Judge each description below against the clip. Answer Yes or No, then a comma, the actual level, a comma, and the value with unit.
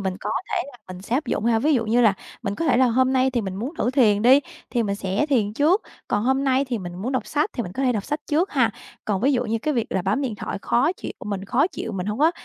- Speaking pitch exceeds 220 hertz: Yes, high, 240 Hz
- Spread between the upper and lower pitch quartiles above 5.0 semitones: No, average, 4.7 semitones